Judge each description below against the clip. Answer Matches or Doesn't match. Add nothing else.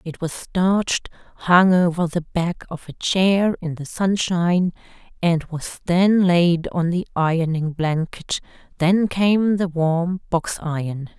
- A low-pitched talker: Doesn't match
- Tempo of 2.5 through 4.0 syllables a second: Matches